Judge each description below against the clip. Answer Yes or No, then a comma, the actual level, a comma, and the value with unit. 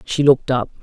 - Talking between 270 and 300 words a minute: No, fast, 220 wpm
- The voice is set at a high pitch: No, low, 130 Hz